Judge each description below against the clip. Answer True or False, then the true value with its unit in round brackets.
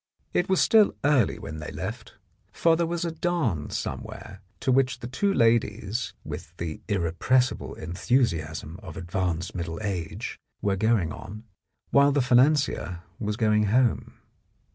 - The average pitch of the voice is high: False (110 Hz)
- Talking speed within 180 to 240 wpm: False (145 wpm)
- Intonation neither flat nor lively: False (6.9 semitones)